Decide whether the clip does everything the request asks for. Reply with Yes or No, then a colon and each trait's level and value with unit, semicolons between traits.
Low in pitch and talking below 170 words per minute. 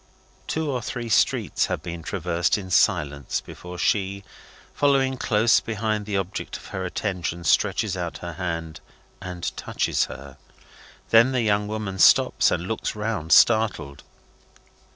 Yes: low, 100 Hz; average, 140 wpm